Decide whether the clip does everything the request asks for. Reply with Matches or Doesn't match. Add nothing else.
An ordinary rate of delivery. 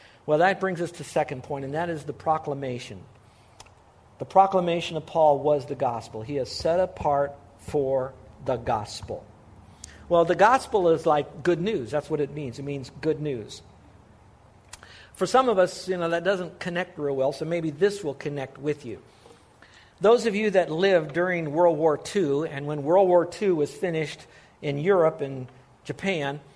Matches